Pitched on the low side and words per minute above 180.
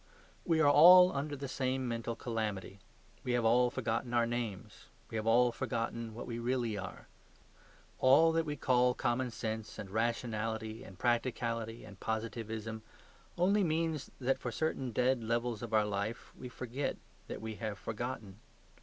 No: low, 120 Hz; average, 160 wpm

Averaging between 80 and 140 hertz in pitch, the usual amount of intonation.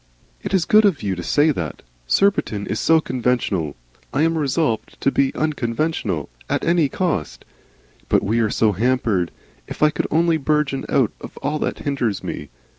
No: low, 135 Hz; wide, 6.8 semitones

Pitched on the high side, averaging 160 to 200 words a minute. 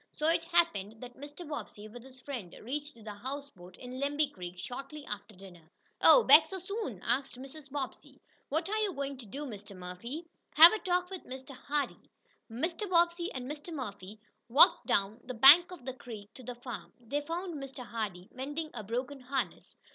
Yes: very high, 270 Hz; average, 185 wpm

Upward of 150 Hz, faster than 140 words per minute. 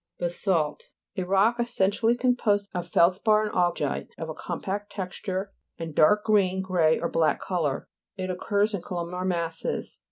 Yes: medium, 185 Hz; average, 155 wpm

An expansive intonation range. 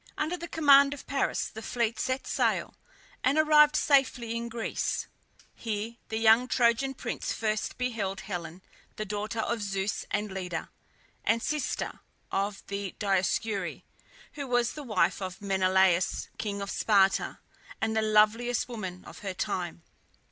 No: average, 4.0 semitones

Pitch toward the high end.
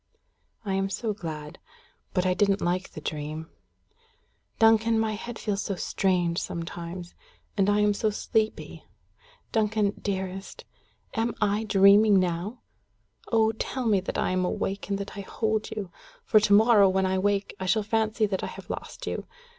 Yes: high, 200 Hz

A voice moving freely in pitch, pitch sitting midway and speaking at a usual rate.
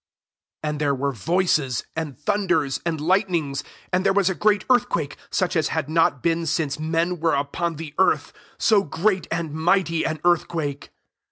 No: average, 3.5 semitones; medium, 165 Hz; average, 170 wpm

